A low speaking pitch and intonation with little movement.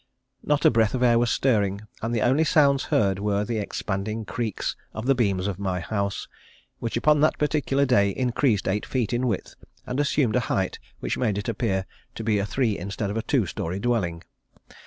No: low, 110 Hz; average, 4.0 semitones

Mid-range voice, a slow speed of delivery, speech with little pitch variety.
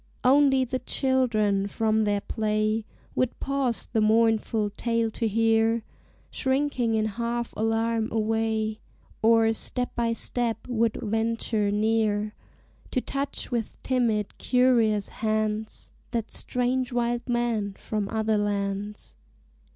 No: high, 225 Hz; slow, 115 wpm; narrow, 1.9 semitones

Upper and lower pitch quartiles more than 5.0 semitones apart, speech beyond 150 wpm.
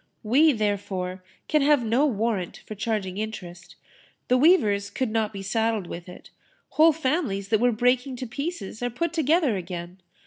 Yes: wide, 5.4 semitones; average, 165 wpm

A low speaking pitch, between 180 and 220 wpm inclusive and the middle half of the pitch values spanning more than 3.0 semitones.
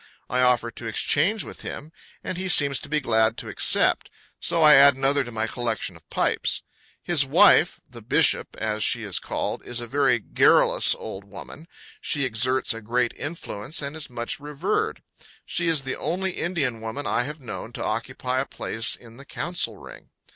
Yes: low, 130 Hz; average, 185 wpm; average, 4.5 semitones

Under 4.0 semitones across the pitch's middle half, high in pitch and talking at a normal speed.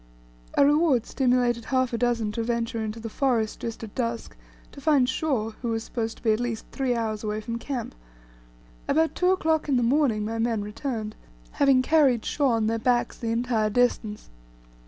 Yes: average, 2.8 semitones; high, 235 Hz; average, 190 wpm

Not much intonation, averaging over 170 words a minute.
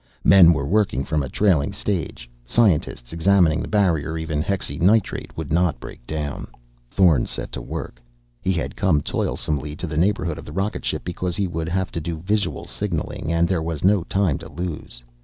No: average, 3.8 semitones; average, 185 wpm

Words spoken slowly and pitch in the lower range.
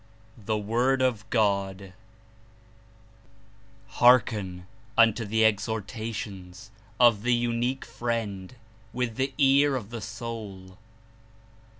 Yes: slow, 90 wpm; low, 110 Hz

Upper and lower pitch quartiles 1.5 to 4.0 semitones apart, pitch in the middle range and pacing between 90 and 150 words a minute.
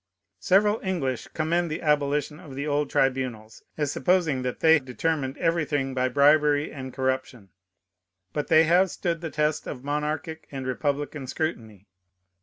Yes: average, 3.3 semitones; medium, 145 Hz; average, 145 wpm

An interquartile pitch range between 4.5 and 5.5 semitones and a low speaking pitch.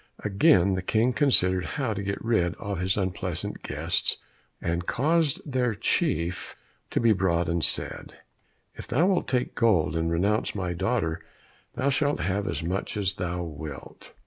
Yes: average, 5.1 semitones; very low, 95 Hz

